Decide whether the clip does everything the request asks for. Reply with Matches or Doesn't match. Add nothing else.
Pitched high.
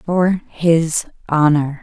Doesn't match